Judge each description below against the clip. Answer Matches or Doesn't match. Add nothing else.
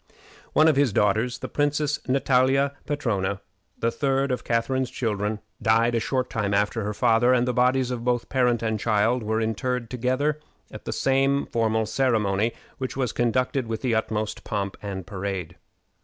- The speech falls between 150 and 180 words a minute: Matches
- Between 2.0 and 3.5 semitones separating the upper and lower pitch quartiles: Matches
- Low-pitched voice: Matches